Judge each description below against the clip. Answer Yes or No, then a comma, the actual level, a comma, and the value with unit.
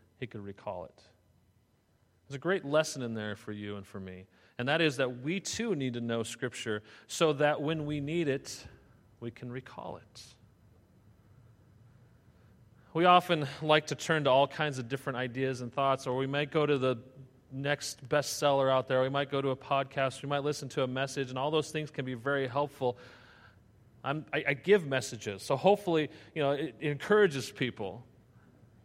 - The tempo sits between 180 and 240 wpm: Yes, average, 190 wpm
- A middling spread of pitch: Yes, average, 4.0 semitones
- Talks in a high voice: No, low, 130 Hz